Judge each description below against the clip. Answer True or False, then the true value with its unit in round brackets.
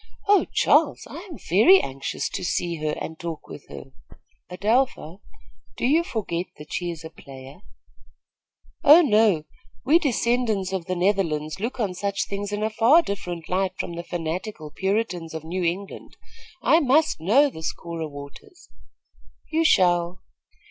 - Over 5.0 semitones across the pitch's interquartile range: True (5.4 semitones)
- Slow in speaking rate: False (155 wpm)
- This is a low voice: False (185 Hz)